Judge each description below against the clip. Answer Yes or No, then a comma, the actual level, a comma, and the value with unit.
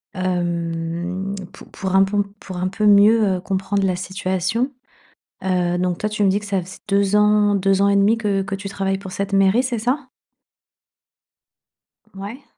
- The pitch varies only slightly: Yes, narrow, 1.8 semitones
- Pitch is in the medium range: No, high, 195 Hz